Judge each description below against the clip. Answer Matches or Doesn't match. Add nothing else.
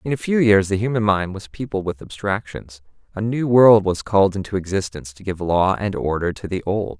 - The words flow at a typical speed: Doesn't match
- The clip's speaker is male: Matches